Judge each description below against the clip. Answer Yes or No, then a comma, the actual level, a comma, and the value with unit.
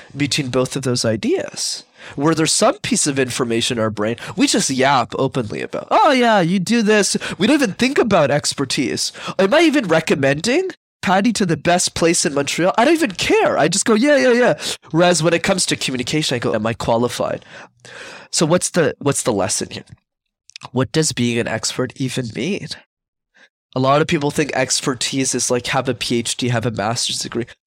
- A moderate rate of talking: Yes, average, 195 wpm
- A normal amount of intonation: No, wide, 7.0 semitones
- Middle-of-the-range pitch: Yes, medium, 145 Hz